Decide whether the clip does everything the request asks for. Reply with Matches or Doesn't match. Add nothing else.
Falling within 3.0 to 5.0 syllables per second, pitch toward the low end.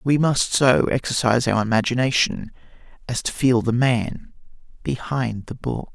Matches